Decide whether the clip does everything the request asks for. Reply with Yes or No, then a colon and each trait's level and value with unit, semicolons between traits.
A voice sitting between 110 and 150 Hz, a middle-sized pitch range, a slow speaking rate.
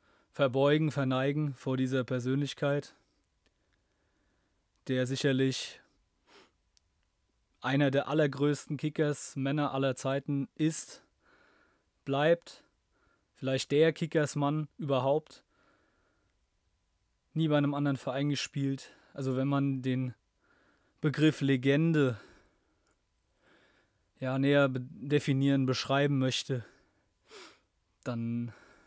No: low, 135 Hz; narrow, 2.2 semitones; slow, 80 wpm